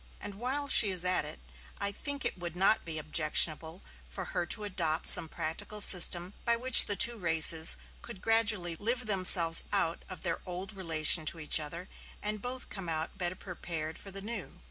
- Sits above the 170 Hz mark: Yes, medium, 185 Hz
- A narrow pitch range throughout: No, average, 4.3 semitones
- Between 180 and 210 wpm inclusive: Yes, average, 190 wpm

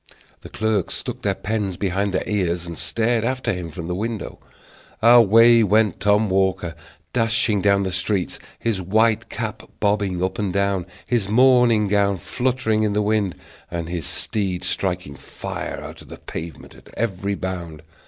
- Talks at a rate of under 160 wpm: No, average, 165 wpm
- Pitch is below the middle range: Yes, low, 100 Hz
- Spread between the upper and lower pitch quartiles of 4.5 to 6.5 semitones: No, average, 3.2 semitones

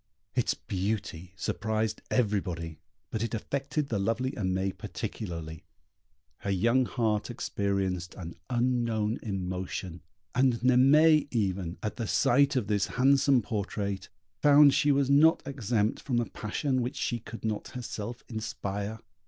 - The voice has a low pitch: Yes, low, 110 Hz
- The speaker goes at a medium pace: No, slow, 130 wpm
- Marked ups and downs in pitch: No, average, 4.5 semitones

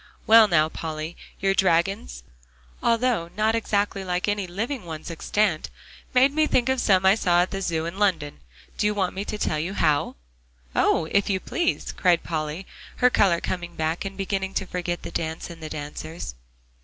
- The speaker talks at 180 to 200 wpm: Yes, average, 185 wpm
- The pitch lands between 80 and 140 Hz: No, medium, 185 Hz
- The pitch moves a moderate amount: Yes, average, 3.9 semitones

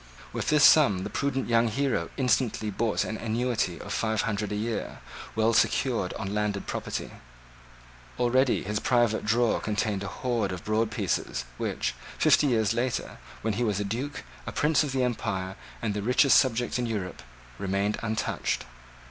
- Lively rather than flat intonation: No, average, 3.2 semitones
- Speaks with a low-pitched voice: Yes, low, 110 Hz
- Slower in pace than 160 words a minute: No, average, 165 wpm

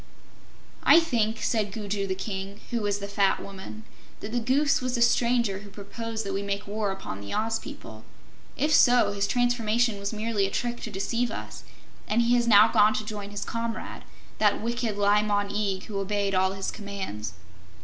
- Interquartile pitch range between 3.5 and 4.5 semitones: No, narrow, 2.6 semitones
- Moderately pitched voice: No, high, 210 Hz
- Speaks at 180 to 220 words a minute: Yes, average, 190 wpm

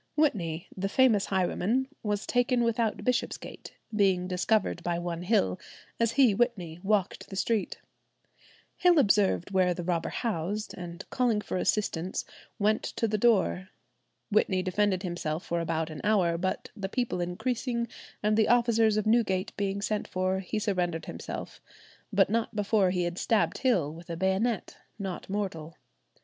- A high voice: Yes, high, 195 Hz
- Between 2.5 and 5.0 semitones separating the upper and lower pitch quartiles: Yes, average, 3.8 semitones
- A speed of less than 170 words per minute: Yes, average, 155 wpm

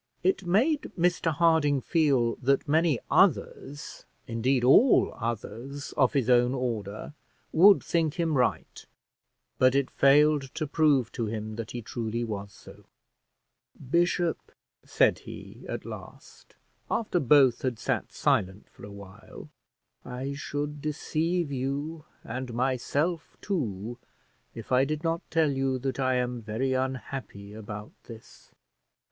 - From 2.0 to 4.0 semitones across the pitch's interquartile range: No, average, 4.5 semitones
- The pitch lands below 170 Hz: Yes, low, 135 Hz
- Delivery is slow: Yes, slow, 130 wpm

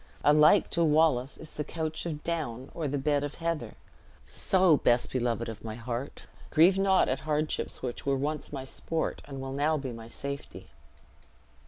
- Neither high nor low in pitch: Yes, medium, 145 Hz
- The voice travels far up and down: No, average, 3.4 semitones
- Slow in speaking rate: No, average, 175 wpm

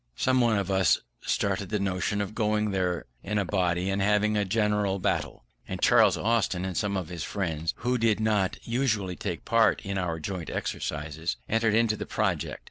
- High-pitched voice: No, low, 100 Hz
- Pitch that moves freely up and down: No, average, 2.8 semitones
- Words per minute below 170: No, average, 190 wpm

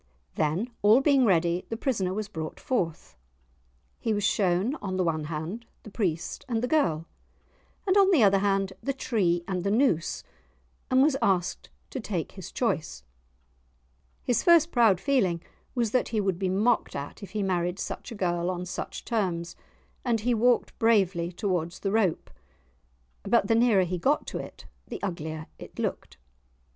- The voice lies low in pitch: No, high, 195 Hz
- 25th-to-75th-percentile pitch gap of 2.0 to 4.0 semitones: No, average, 5.2 semitones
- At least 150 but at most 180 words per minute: Yes, average, 170 wpm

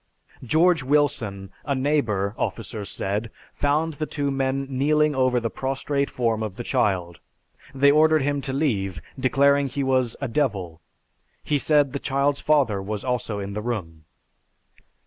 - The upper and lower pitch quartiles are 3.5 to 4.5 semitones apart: No, average, 5.2 semitones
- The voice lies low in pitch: Yes, low, 130 Hz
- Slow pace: No, average, 145 wpm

